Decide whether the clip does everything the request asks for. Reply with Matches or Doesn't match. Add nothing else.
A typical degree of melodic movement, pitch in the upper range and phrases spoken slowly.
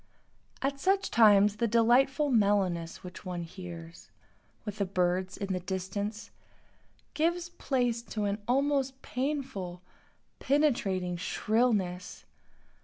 Doesn't match